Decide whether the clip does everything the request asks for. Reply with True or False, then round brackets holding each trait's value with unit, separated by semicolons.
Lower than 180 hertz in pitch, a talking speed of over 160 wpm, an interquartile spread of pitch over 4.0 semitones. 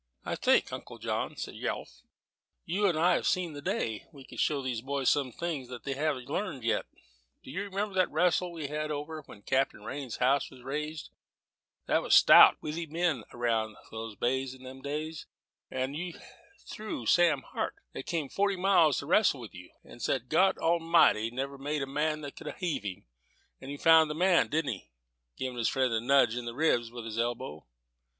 True (140 Hz; 195 wpm; 4.6 semitones)